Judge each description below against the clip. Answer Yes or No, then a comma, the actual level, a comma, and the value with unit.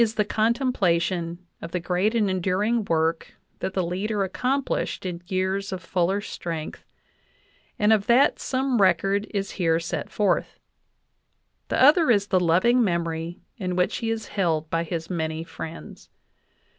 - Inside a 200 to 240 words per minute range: No, average, 145 wpm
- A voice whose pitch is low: No, medium, 185 Hz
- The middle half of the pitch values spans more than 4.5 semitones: No, average, 4.0 semitones